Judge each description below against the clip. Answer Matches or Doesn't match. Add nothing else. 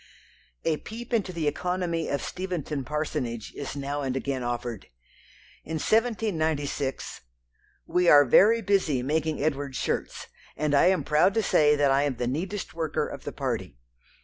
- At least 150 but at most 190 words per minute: Matches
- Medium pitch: Matches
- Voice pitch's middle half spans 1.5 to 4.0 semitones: Doesn't match